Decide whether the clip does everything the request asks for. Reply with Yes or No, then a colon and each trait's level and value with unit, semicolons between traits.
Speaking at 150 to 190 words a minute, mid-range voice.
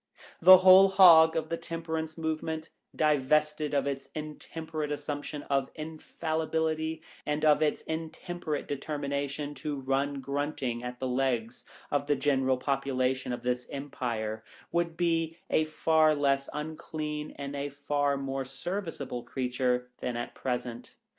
No: average, 140 wpm; medium, 145 Hz